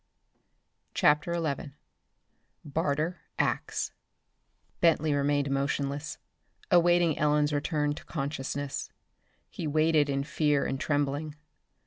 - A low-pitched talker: No, medium, 150 Hz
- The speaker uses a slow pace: Yes, slow, 90 wpm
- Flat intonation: Yes, narrow, 1.7 semitones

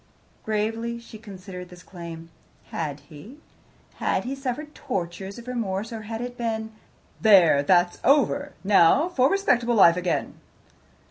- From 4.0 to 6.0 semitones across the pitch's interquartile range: Yes, average, 5.3 semitones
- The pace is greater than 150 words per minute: No, slow, 135 wpm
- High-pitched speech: Yes, high, 215 Hz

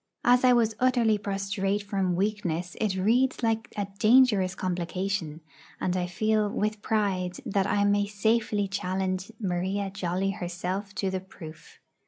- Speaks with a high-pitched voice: Yes, high, 200 Hz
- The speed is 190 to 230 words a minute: No, average, 145 wpm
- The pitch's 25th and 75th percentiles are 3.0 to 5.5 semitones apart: No, narrow, 2.6 semitones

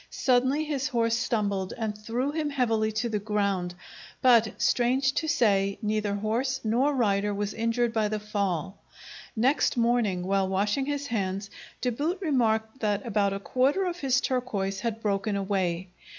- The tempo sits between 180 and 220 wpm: No, average, 160 wpm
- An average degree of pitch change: Yes, average, 4.1 semitones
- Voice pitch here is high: Yes, high, 220 Hz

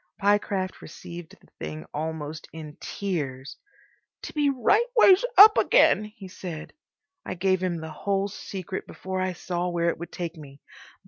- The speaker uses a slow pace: No, average, 155 wpm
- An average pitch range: Yes, average, 3.9 semitones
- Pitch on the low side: No, medium, 180 Hz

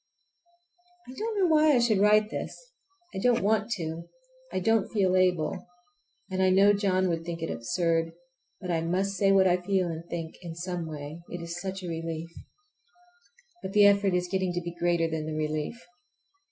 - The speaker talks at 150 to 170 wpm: No, average, 185 wpm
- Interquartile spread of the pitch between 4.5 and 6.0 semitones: No, average, 3.1 semitones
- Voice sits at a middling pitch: Yes, medium, 180 Hz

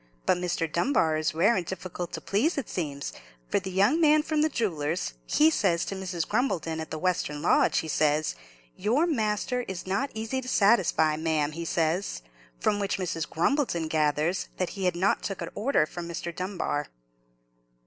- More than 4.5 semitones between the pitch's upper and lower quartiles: Yes, average, 5.0 semitones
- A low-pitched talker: No, medium, 185 Hz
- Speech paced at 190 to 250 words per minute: No, average, 180 wpm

